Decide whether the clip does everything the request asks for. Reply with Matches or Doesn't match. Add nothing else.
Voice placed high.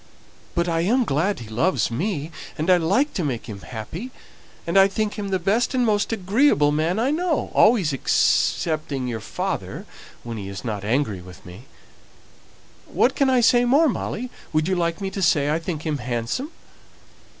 Doesn't match